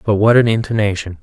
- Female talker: No, male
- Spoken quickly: No, average, 195 wpm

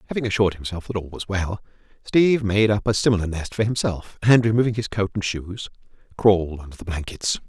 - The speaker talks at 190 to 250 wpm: Yes, average, 200 wpm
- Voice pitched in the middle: No, low, 100 Hz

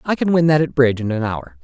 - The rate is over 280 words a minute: Yes, fast, 330 wpm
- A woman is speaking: No, male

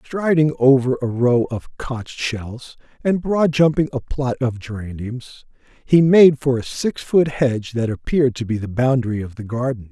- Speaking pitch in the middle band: No, low, 130 Hz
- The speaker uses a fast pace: No, average, 180 wpm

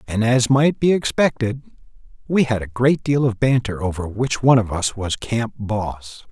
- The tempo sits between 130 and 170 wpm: No, average, 190 wpm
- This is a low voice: Yes, low, 115 Hz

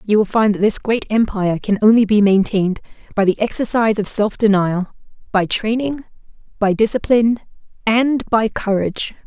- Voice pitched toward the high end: Yes, high, 215 Hz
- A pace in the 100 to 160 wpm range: Yes, average, 155 wpm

